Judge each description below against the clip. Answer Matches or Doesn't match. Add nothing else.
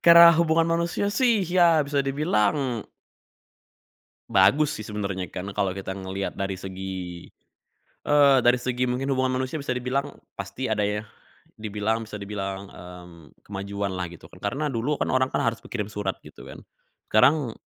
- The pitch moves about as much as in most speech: Doesn't match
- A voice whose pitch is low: Matches